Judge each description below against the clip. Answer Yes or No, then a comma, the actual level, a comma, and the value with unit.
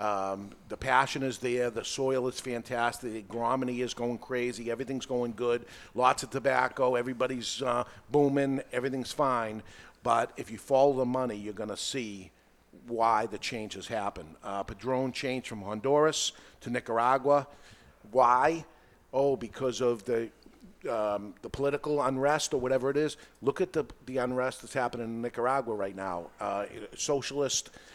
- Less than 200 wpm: Yes, average, 150 wpm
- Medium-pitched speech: No, low, 125 Hz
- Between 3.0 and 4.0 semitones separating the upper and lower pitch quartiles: No, narrow, 2.6 semitones